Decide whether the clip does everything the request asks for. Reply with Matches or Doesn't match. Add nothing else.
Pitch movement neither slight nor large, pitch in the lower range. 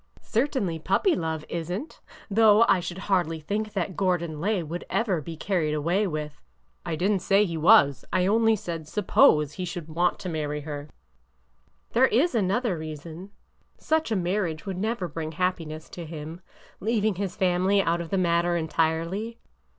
Doesn't match